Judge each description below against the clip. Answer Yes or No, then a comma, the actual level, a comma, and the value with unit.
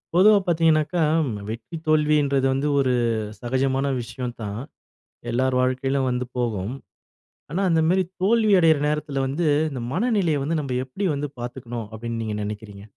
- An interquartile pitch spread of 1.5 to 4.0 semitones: No, average, 4.8 semitones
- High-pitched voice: No, low, 135 Hz